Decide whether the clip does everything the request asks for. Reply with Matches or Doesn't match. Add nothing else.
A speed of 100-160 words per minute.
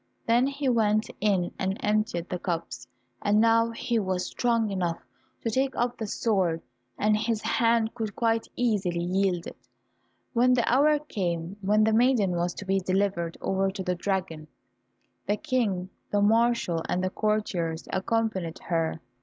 Matches